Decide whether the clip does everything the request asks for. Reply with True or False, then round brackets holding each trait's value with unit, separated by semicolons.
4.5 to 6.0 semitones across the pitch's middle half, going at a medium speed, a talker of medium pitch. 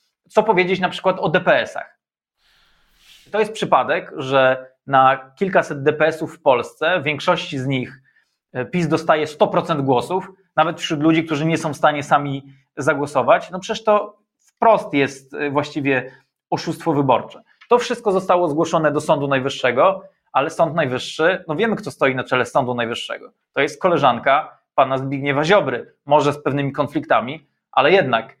True (4.9 semitones; 150 wpm; 155 Hz)